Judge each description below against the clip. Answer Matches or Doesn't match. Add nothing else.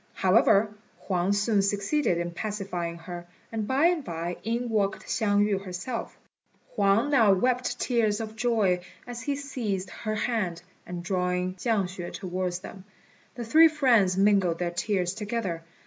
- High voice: Matches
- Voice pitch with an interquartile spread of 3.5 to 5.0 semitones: Matches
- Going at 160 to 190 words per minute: Doesn't match